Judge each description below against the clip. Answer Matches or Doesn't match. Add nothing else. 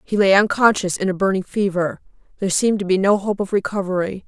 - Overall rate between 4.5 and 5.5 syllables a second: Doesn't match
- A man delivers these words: Doesn't match